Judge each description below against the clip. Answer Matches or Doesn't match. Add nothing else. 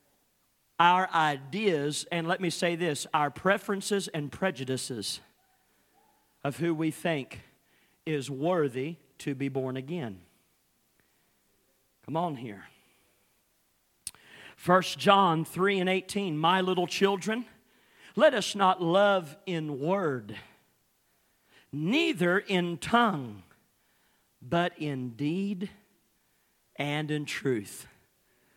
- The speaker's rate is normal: Doesn't match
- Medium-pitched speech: Matches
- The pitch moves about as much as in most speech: Matches